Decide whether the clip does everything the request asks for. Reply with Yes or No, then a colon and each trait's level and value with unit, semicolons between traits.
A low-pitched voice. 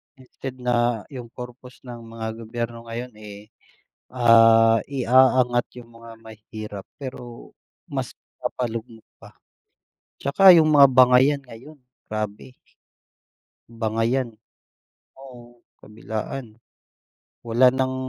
Yes: low, 120 Hz